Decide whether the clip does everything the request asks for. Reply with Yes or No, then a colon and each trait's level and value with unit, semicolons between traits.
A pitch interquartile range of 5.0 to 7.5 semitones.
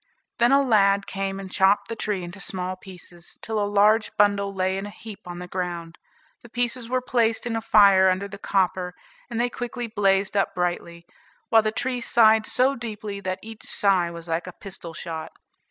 No: average, 3.2 semitones